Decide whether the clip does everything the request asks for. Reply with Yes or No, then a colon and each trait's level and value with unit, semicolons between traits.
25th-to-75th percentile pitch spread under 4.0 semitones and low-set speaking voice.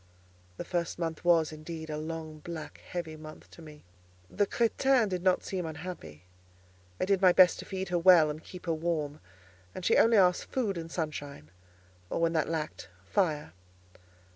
No: average, 2.9 semitones; medium, 165 Hz